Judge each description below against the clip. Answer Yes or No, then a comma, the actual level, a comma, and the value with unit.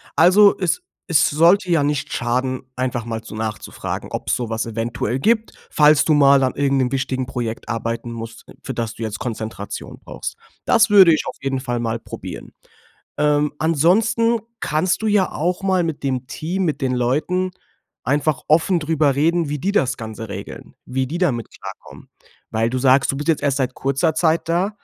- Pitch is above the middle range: No, medium, 140 Hz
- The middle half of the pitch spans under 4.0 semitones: No, wide, 5.4 semitones